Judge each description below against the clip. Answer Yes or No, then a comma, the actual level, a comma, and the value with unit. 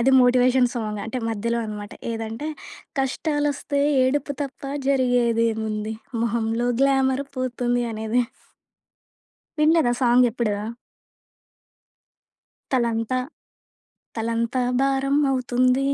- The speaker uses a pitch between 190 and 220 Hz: No, high, 245 Hz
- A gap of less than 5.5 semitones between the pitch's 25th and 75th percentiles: Yes, average, 2.7 semitones